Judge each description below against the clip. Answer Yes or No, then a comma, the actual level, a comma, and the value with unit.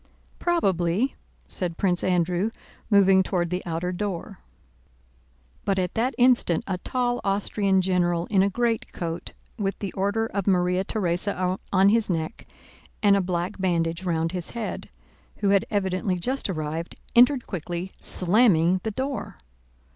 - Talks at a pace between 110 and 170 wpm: Yes, average, 140 wpm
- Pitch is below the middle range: No, high, 190 Hz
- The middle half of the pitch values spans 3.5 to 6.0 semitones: No, average, 2.8 semitones